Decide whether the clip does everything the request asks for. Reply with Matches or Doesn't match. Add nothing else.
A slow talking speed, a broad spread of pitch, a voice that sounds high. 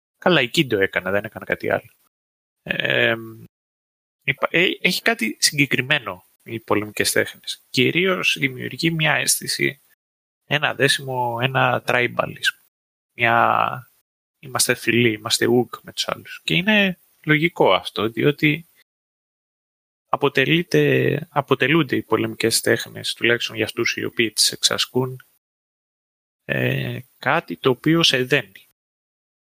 Doesn't match